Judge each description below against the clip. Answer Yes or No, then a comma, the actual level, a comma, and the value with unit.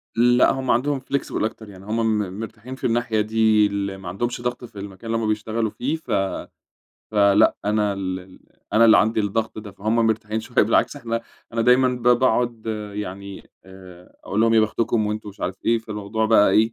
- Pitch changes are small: Yes, narrow, 2.2 semitones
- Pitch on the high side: No, low, 110 Hz